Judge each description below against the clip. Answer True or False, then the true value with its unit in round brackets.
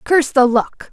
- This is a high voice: True (270 Hz)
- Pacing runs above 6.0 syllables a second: False (4.9 syllables/s)